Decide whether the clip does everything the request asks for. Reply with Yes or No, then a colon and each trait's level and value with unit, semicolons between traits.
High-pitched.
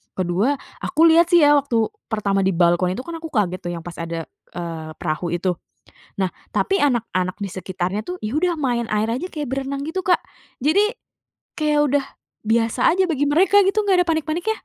Yes: very high, 255 Hz